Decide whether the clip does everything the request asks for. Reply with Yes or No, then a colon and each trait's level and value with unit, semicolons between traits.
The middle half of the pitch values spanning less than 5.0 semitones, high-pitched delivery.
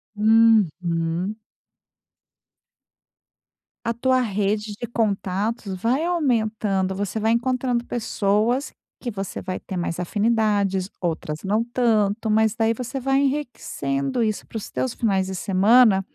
Yes: average, 3.5 semitones; high, 215 Hz